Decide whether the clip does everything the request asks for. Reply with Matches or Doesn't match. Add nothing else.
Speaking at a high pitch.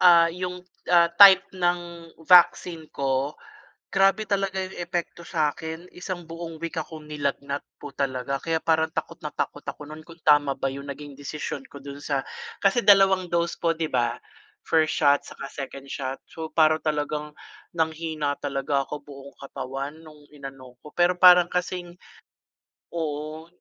Doesn't match